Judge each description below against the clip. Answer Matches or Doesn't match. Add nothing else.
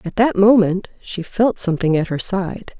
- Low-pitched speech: Doesn't match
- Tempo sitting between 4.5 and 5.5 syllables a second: Matches